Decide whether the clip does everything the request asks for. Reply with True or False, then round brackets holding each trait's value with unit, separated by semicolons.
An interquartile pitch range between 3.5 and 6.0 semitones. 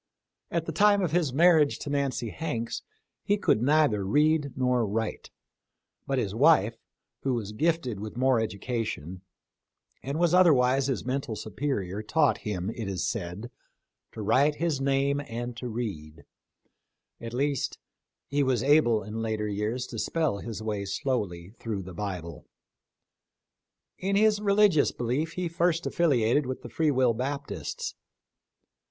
True (5.6 semitones)